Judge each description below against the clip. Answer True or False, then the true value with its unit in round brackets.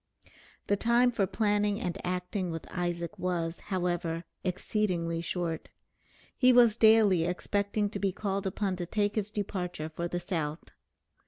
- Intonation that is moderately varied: True (3.1 semitones)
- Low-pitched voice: False (185 Hz)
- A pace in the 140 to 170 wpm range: True (145 wpm)